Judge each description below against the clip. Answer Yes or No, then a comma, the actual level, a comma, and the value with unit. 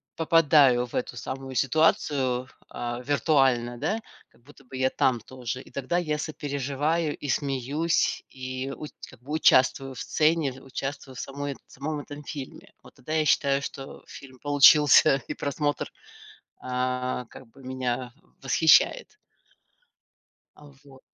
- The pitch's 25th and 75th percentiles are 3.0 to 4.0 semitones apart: No, narrow, 2.5 semitones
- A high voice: No, low, 135 Hz